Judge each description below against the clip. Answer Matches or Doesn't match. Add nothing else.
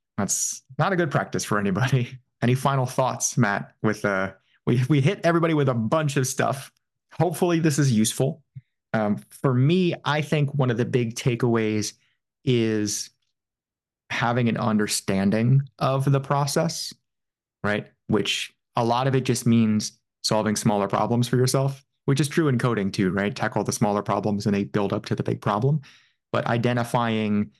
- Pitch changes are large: Doesn't match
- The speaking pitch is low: Matches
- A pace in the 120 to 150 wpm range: Doesn't match